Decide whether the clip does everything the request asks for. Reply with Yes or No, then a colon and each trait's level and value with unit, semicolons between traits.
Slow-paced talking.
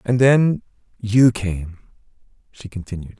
Yes: slow, 115 wpm